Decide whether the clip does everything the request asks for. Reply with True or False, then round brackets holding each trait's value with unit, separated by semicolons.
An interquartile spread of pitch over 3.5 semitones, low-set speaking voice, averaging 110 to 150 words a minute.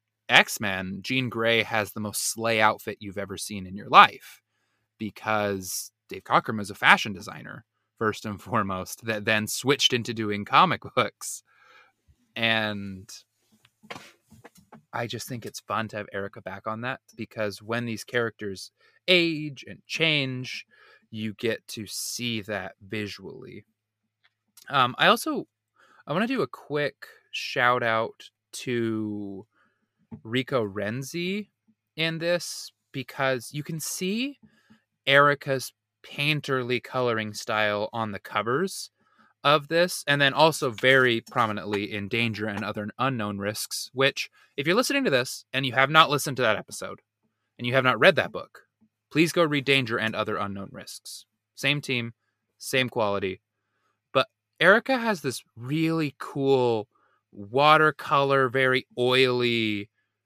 True (4.2 semitones; 115 Hz; 135 wpm)